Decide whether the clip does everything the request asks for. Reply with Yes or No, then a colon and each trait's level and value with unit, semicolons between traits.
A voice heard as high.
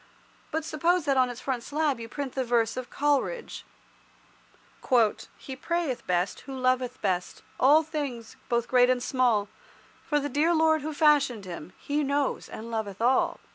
Yes: very high, 260 Hz